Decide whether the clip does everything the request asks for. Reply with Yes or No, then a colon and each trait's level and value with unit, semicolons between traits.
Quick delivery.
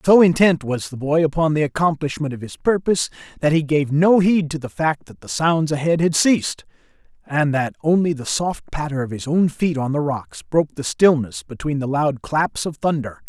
Yes: fast, 210 wpm